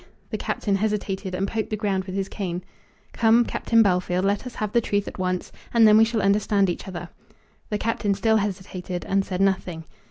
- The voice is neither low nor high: No, high, 200 Hz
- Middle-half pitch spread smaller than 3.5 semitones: Yes, narrow, 2.4 semitones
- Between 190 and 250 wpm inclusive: Yes, average, 200 wpm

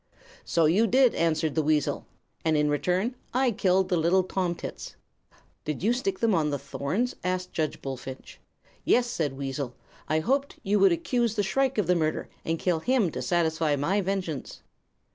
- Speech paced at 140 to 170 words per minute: No, average, 180 wpm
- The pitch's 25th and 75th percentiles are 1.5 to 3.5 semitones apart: No, average, 4.9 semitones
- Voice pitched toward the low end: No, medium, 175 Hz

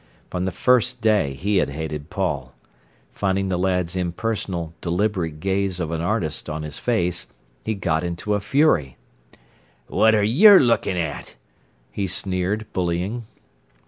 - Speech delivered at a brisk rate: No, average, 145 wpm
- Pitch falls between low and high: No, very low, 95 Hz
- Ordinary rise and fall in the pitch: Yes, average, 4.0 semitones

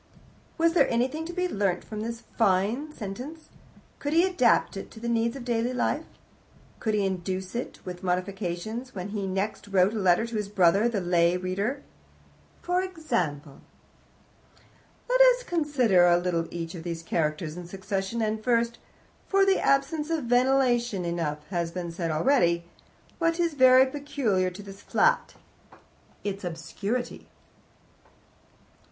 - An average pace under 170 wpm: Yes, average, 150 wpm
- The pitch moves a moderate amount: No, wide, 6.5 semitones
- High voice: Yes, high, 215 Hz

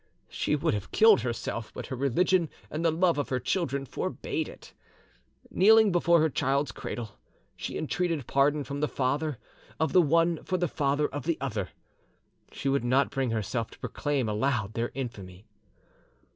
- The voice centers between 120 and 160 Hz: Yes, medium, 140 Hz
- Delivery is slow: No, average, 170 wpm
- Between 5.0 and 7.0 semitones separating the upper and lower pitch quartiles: Yes, average, 5.3 semitones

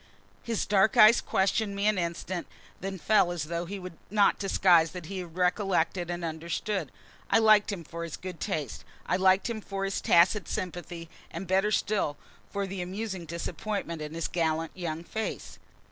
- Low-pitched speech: No, medium, 185 Hz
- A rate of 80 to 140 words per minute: No, average, 175 wpm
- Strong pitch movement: No, average, 3.0 semitones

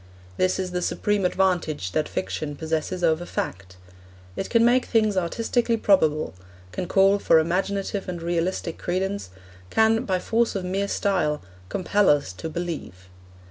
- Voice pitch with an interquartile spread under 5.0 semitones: Yes, average, 3.9 semitones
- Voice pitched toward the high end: No, medium, 180 Hz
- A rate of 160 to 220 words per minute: No, average, 145 wpm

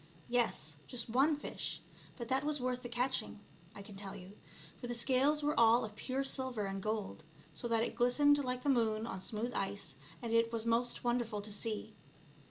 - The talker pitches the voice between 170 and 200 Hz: No, high, 235 Hz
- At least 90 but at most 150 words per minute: No, average, 195 wpm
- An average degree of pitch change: Yes, average, 3.0 semitones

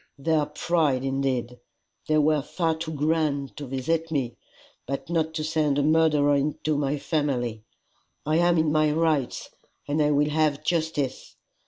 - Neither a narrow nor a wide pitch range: No, narrow, 2.3 semitones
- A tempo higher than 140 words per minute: Yes, average, 155 wpm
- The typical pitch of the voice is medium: Yes, medium, 150 Hz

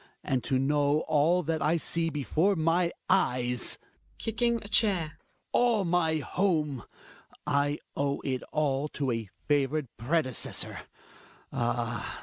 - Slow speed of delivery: Yes, slow, 130 wpm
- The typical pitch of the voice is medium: Yes, medium, 150 Hz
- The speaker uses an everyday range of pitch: Yes, average, 4.0 semitones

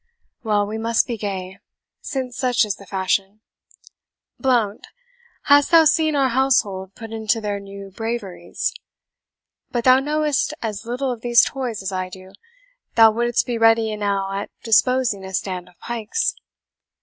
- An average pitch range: Yes, average, 4.0 semitones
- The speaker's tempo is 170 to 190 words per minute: No, average, 150 wpm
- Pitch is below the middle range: No, high, 225 Hz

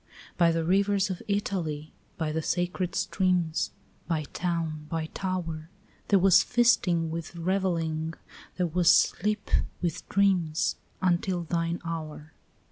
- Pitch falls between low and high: Yes, medium, 170 Hz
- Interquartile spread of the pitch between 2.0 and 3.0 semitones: Yes, narrow, 2.5 semitones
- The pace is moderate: No, slow, 125 wpm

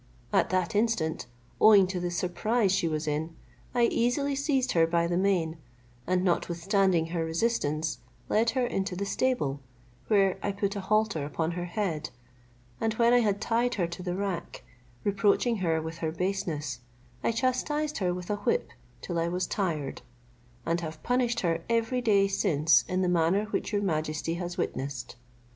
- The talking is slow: No, average, 170 wpm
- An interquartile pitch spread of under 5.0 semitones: Yes, average, 4.6 semitones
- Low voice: No, medium, 185 Hz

